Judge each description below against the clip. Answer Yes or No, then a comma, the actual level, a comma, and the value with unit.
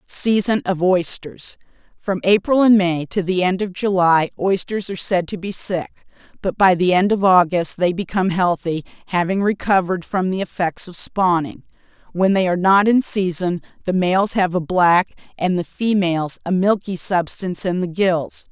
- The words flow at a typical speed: Yes, average, 170 wpm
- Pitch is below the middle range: No, medium, 185 Hz